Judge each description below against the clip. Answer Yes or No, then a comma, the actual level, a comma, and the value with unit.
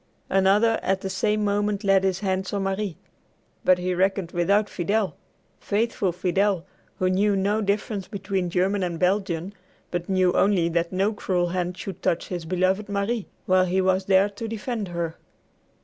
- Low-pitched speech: No, high, 190 Hz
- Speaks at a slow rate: No, average, 165 wpm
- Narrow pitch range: Yes, narrow, 1.9 semitones